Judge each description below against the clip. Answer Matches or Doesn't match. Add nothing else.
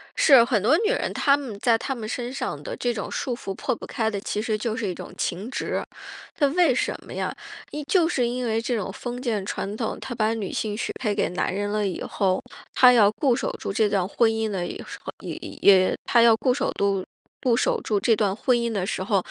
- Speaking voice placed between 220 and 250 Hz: Matches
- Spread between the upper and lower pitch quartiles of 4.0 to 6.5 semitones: Doesn't match